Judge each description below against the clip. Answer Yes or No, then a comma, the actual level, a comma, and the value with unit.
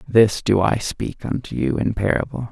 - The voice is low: Yes, low, 105 Hz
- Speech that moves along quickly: No, average, 190 wpm